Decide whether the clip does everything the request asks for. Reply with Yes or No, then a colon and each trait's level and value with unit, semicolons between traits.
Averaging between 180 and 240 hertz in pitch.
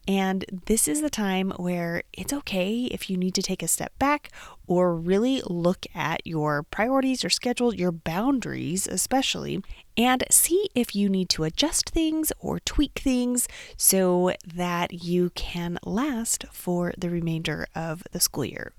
Yes: high, 190 Hz